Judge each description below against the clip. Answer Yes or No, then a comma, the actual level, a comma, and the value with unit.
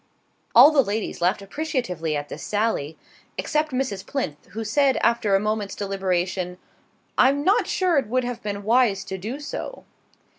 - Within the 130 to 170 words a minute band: Yes, average, 160 wpm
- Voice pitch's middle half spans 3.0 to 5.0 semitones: No, wide, 5.5 semitones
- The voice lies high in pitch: Yes, high, 215 Hz